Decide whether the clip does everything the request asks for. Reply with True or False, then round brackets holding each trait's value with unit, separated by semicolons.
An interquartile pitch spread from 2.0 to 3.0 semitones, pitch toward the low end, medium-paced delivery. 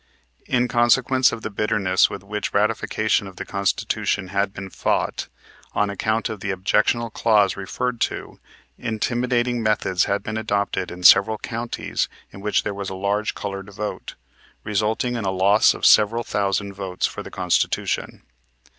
True (2.4 semitones; 105 Hz; 160 wpm)